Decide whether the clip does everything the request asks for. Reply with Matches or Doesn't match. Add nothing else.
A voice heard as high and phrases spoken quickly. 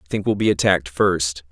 Doesn't match